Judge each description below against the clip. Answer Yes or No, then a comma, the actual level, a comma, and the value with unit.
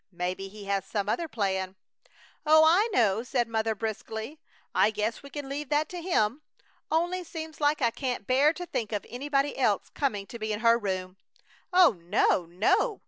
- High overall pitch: Yes, high, 230 Hz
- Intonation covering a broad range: Yes, wide, 6.6 semitones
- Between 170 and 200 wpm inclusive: Yes, average, 185 wpm